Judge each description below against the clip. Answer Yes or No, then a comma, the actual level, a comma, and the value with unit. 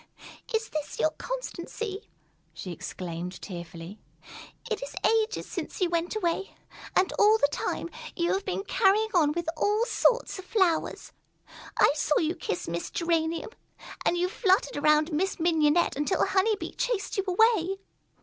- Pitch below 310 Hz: No, very high, 350 Hz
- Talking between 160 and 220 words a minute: No, average, 150 wpm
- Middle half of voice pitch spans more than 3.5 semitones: Yes, average, 5.3 semitones